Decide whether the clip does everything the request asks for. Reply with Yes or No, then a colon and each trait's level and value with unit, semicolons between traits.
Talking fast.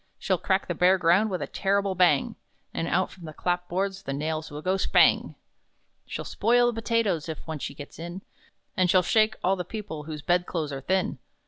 Yes: fast, 210 wpm